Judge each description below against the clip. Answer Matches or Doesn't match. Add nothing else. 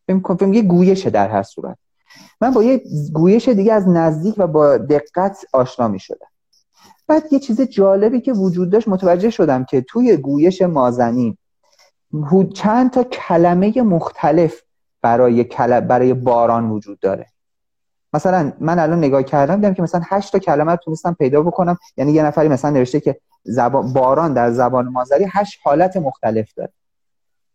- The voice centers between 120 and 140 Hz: Doesn't match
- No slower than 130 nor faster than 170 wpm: Matches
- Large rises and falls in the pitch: Matches